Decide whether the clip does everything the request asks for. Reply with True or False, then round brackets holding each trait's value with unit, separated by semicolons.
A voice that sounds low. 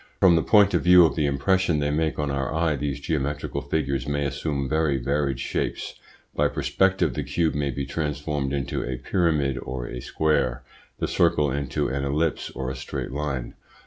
True (70 Hz)